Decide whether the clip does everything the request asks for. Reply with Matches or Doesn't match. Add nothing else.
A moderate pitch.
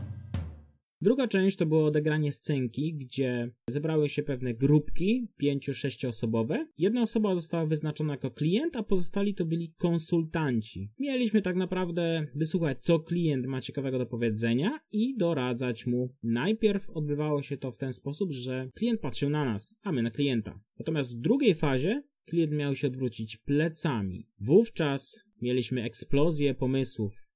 Matches